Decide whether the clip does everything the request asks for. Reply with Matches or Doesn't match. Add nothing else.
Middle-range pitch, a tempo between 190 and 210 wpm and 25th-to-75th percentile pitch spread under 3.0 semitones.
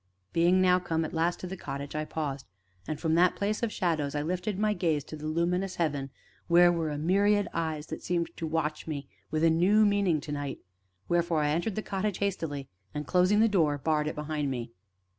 Doesn't match